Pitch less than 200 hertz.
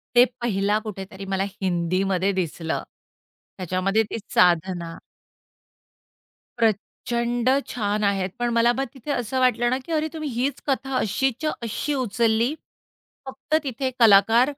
No: high, 225 Hz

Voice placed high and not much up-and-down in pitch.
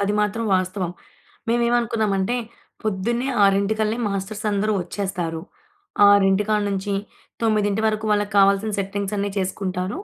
Yes: high, 200 Hz; narrow, 1.9 semitones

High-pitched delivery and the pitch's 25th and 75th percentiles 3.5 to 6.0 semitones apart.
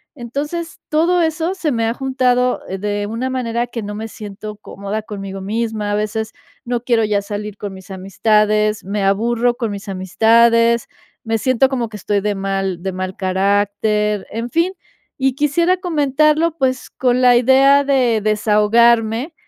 Yes: high, 225 Hz; average, 3.9 semitones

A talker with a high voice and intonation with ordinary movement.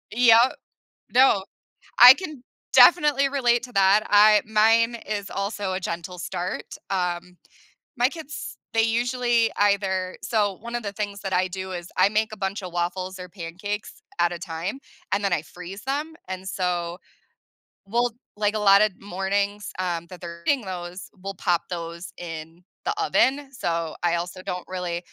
Yes: high, 195 Hz; average, 3.9 semitones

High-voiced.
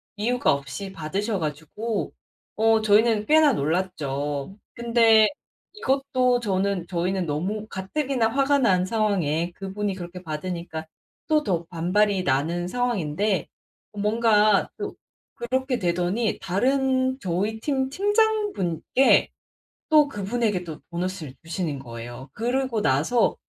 Yes: high, 205 Hz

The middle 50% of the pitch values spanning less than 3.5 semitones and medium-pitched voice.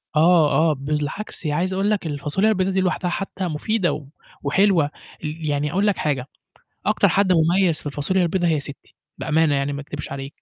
No: average, 4.2 semitones; medium, 160 Hz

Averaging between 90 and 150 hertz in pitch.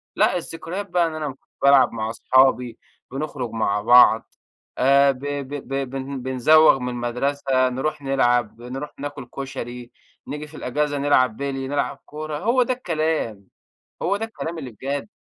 Yes: low, 135 Hz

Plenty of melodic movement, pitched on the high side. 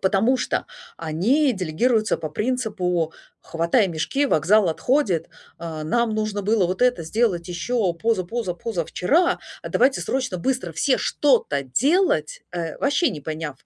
Yes: wide, 7.0 semitones; high, 200 Hz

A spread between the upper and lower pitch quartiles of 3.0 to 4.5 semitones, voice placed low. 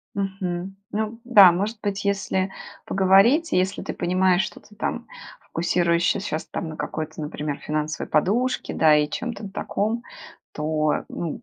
No: average, 4.2 semitones; high, 190 Hz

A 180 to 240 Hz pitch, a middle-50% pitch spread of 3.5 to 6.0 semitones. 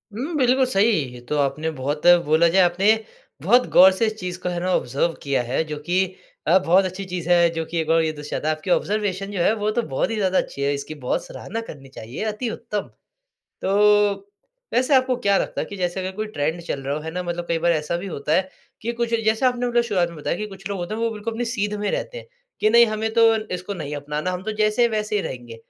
Yes: medium, 185 Hz; average, 5.3 semitones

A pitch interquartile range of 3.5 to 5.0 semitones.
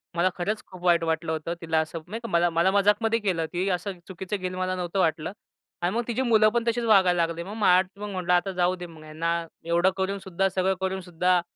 No: narrow, 2.6 semitones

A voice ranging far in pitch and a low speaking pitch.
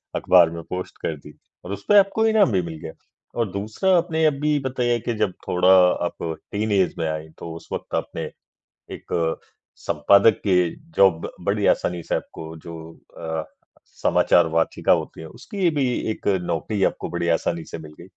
Yes: wide, 6.6 semitones; very low, 95 Hz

